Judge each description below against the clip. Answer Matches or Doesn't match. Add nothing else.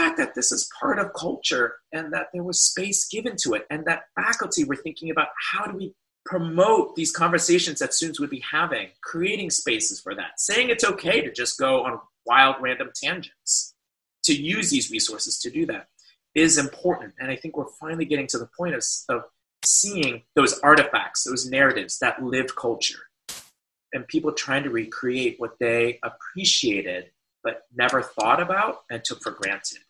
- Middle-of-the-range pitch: Matches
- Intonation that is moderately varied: Doesn't match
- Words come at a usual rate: Matches